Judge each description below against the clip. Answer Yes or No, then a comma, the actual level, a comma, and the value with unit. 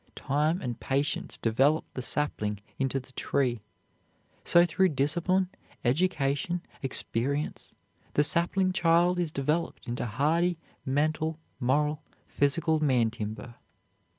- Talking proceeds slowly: Yes, slow, 110 wpm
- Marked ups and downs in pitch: No, average, 4.2 semitones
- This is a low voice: No, medium, 145 Hz